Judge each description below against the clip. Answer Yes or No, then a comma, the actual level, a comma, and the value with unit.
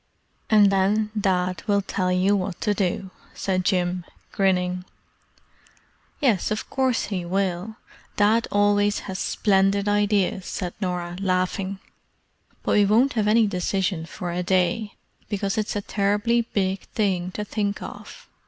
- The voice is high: Yes, high, 195 Hz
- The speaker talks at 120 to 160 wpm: Yes, average, 140 wpm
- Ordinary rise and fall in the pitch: No, narrow, 2.2 semitones